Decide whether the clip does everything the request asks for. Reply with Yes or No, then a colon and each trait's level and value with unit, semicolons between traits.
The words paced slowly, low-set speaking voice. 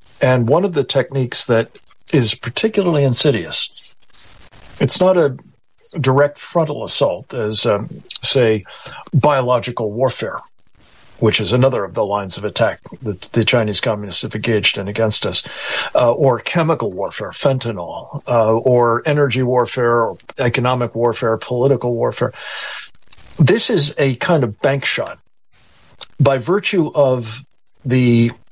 Yes: slow, 130 wpm; low, 125 Hz